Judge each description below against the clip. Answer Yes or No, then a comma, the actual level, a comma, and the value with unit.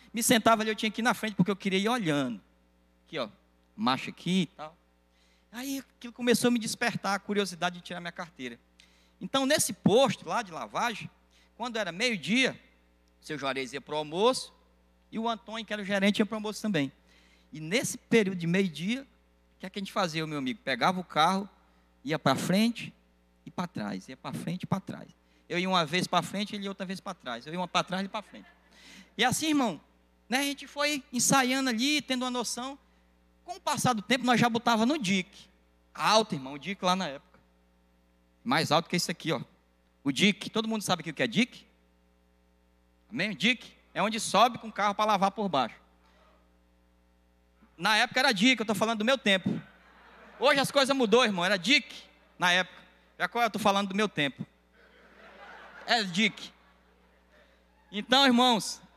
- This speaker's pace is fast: Yes, fast, 195 wpm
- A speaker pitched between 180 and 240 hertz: Yes, high, 190 Hz